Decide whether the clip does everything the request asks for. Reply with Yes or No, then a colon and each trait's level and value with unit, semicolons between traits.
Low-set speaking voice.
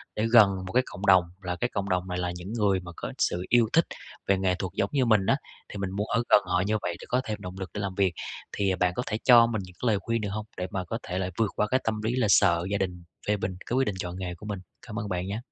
Yes: low, 100 Hz